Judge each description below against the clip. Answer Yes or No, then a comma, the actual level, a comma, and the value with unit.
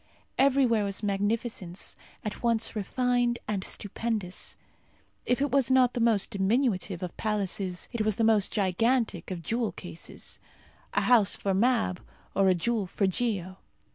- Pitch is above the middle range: Yes, high, 215 Hz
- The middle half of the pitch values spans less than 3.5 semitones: No, average, 3.8 semitones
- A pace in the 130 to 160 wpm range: Yes, average, 145 wpm